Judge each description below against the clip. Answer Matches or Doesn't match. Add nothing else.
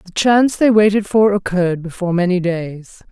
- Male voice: Doesn't match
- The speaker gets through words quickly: Doesn't match